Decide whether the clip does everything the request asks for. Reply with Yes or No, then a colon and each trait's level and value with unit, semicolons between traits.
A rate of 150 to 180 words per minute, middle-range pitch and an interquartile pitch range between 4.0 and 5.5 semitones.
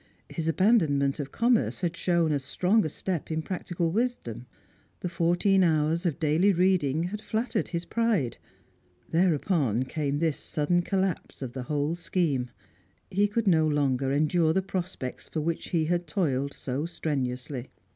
Yes: average, 155 wpm; medium, 165 Hz; average, 4.3 semitones